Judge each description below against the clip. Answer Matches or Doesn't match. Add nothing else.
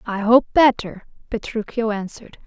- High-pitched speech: Matches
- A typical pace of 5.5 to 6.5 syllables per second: Doesn't match